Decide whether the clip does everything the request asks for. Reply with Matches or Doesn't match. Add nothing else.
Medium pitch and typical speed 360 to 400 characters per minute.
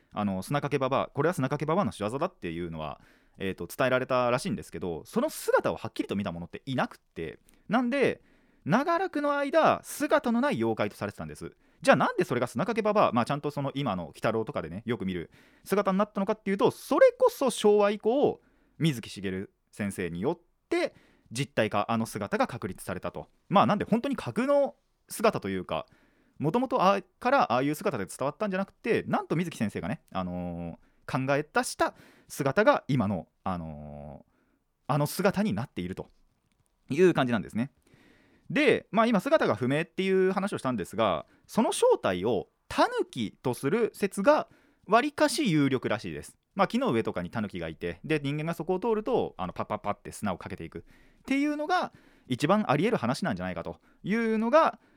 Matches